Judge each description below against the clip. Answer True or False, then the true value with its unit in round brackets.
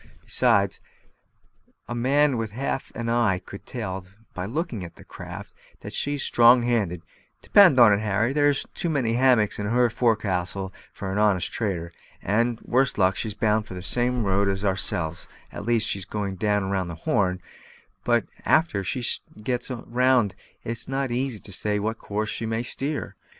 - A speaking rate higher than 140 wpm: True (165 wpm)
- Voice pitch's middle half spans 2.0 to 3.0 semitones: False (4.0 semitones)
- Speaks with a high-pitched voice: False (110 Hz)